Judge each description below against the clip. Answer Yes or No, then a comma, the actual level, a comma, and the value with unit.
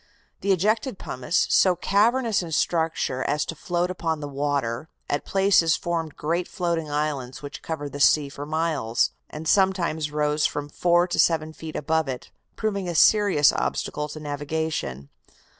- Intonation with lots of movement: No, average, 3.3 semitones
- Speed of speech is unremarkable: Yes, average, 160 wpm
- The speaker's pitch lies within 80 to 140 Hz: No, medium, 160 Hz